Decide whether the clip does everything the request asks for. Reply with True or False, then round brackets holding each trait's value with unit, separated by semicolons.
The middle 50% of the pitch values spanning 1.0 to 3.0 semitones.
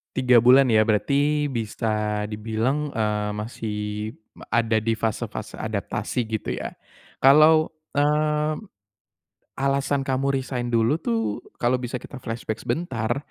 False (4.1 semitones)